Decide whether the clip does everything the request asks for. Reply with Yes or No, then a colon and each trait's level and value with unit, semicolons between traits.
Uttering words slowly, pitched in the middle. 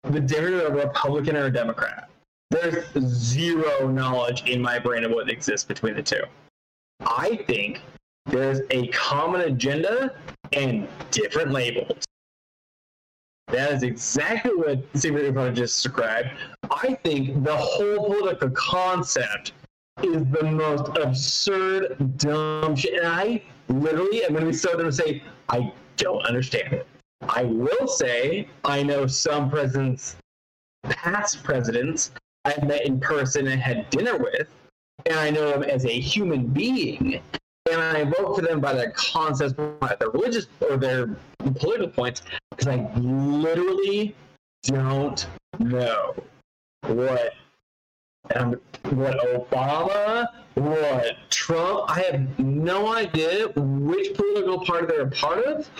Yes: slow, 130 wpm; medium, 145 Hz